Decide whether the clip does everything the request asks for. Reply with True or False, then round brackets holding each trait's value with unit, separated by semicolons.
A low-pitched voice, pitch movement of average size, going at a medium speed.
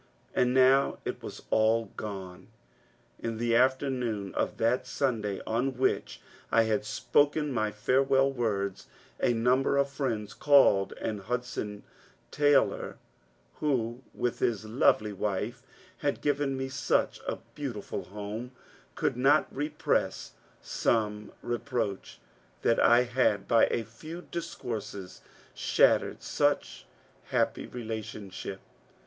False (120 Hz; 3.8 semitones; 125 wpm)